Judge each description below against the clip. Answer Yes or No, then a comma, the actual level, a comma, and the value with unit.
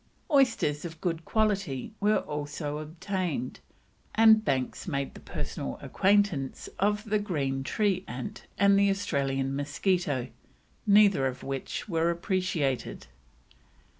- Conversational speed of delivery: No, slow, 115 wpm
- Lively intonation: Yes, wide, 6.5 semitones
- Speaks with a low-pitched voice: No, medium, 170 Hz